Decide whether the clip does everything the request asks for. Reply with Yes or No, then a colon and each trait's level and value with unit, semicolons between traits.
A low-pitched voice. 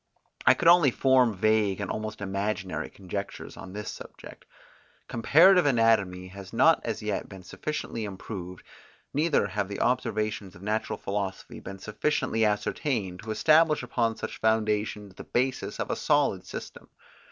Yes: low, 110 Hz